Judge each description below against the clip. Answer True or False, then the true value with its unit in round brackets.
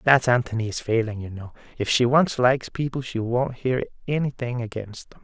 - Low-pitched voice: True (120 Hz)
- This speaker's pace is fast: False (185 wpm)